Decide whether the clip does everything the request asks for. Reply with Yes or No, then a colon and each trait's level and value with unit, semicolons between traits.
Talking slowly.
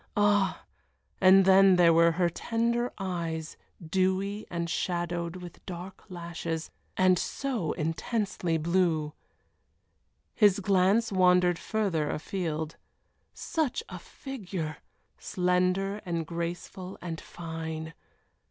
Yes: slow, 100 wpm